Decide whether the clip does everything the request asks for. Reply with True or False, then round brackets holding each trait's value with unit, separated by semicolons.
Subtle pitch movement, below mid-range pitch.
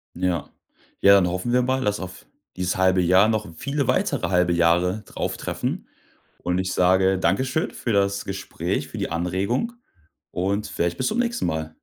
False (3.4 semitones; 95 Hz)